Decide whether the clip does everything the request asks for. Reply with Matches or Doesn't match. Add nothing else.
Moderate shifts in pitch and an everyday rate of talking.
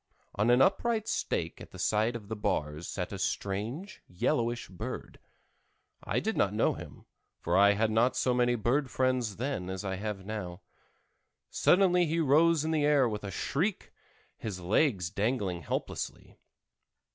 Doesn't match